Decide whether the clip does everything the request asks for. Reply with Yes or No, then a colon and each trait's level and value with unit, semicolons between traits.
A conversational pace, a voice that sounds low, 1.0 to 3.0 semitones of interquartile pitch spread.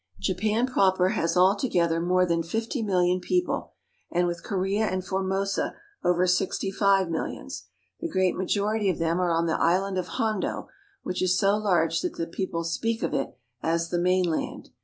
No: average, 175 wpm; medium, 185 Hz; narrow, 2.5 semitones